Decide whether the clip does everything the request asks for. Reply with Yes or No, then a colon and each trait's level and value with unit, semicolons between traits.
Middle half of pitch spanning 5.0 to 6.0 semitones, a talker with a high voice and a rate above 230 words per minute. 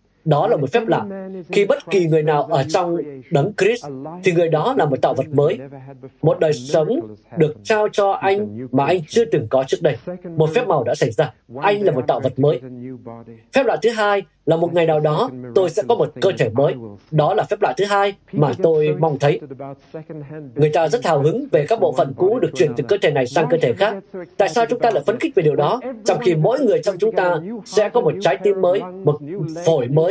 No: wide, 5.5 semitones; medium, 165 Hz; average, 240 wpm